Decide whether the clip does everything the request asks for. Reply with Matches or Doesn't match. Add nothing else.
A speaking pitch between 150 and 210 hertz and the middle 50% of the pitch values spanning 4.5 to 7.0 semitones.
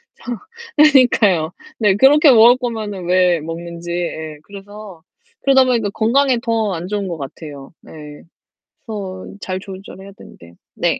Matches